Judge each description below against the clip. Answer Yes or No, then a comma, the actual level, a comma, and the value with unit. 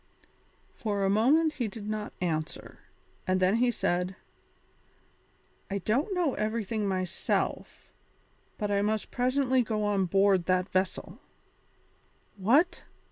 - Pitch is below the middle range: No, high, 210 Hz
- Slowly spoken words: Yes, slow, 120 wpm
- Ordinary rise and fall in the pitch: Yes, average, 4.2 semitones